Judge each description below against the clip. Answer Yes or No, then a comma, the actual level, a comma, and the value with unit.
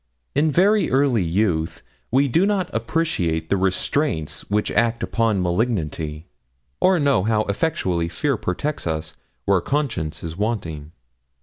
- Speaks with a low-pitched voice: Yes, low, 105 Hz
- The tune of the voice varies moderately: No, wide, 9.0 semitones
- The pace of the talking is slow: Yes, slow, 130 wpm